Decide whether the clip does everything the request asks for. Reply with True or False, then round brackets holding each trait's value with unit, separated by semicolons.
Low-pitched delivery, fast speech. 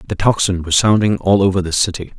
True (95 Hz; 220 wpm)